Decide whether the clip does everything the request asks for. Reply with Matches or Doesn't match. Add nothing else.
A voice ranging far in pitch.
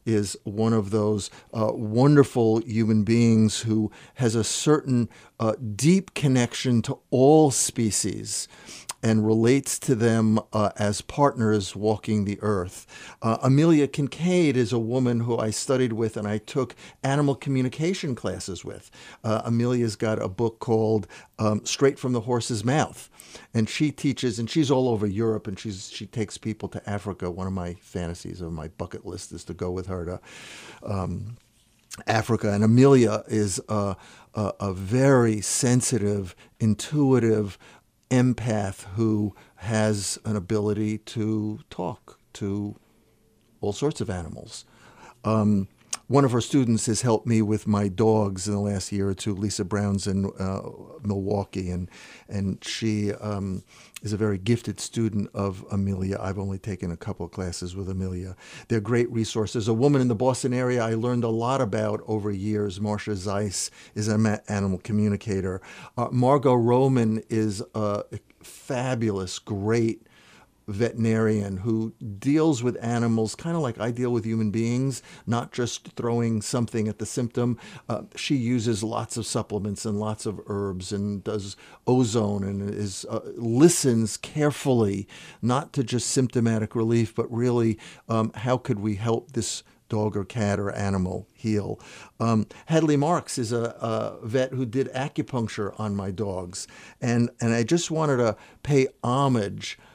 Doesn't match